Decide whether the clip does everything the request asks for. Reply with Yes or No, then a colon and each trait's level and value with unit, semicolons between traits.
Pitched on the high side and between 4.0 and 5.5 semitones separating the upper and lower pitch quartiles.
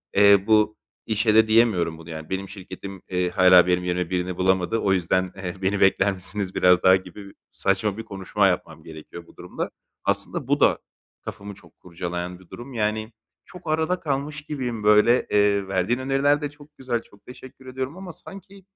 No: low, 100 Hz; average, 5.0 semitones